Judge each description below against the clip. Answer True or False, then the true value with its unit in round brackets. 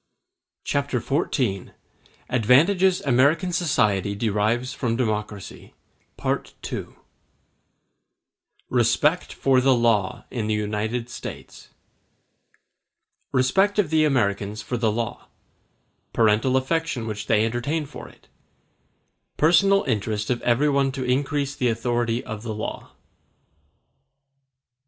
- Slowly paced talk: True (95 wpm)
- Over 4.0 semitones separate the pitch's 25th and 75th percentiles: True (4.5 semitones)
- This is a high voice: False (120 Hz)